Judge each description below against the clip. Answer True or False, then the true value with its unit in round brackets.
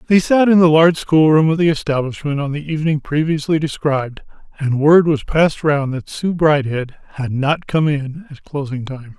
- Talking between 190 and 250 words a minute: True (195 wpm)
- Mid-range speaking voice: True (150 Hz)